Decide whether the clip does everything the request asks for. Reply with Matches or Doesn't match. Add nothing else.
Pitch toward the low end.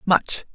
Doesn't match